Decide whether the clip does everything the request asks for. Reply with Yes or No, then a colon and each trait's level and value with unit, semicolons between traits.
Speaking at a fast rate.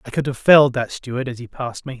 Yes: fast, 300 wpm